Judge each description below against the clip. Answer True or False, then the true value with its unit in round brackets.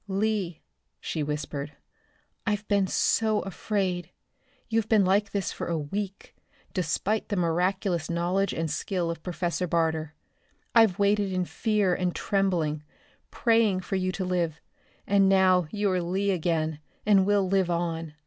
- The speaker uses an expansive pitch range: False (3.0 semitones)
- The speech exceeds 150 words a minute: False (145 wpm)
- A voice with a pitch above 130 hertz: True (185 Hz)